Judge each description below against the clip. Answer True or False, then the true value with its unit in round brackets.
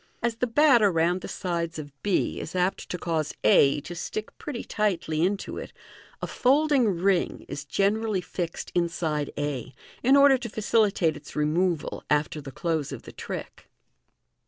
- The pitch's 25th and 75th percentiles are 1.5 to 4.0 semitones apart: False (5.5 semitones)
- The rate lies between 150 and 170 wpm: True (160 wpm)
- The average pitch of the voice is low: False (180 Hz)